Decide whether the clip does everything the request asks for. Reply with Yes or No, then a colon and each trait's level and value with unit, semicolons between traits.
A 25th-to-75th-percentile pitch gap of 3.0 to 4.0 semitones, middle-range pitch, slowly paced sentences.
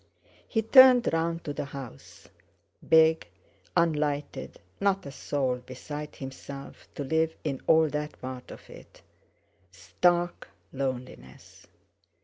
Yes: average, 3.7 semitones; medium, 150 Hz; slow, 115 wpm